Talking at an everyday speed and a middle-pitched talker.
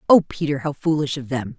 No: fast, 225 wpm; medium, 145 Hz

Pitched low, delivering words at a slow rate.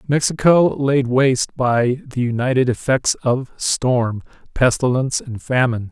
Yes: low, 130 Hz; slow, 120 wpm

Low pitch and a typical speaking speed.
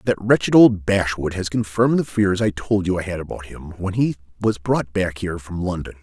No: very low, 95 Hz; fast, 230 wpm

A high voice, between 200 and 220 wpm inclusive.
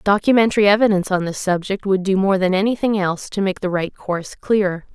Yes: high, 195 Hz; fast, 205 wpm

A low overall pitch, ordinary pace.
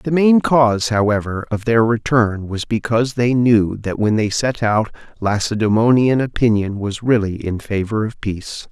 Yes: low, 110 Hz; average, 165 wpm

